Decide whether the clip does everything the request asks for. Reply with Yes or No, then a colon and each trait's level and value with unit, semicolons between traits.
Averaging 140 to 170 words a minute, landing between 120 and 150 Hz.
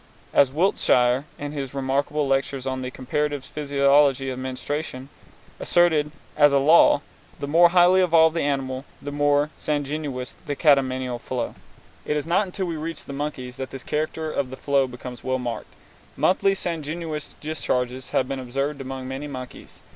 Yes: average, 160 wpm; medium, 140 Hz